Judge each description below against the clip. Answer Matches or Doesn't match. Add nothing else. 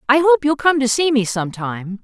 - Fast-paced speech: Matches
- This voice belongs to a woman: Matches